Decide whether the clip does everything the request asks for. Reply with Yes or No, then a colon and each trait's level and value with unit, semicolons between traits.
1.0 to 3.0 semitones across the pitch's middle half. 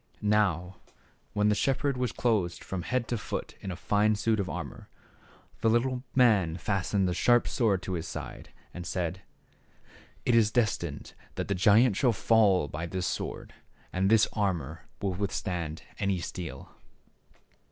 No: average, 4.1 semitones